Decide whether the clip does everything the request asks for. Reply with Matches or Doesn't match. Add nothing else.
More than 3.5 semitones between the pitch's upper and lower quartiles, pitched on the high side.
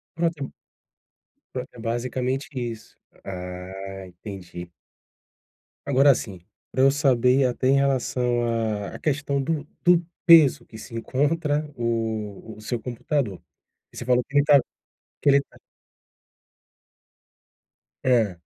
Doesn't match